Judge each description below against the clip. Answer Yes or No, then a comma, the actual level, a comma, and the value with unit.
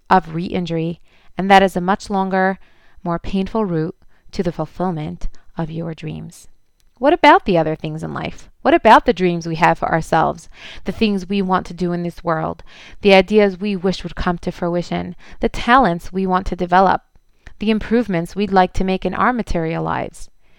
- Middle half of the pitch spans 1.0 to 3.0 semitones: Yes, average, 2.7 semitones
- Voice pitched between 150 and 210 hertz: Yes, medium, 185 Hz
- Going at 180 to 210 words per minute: Yes, average, 190 wpm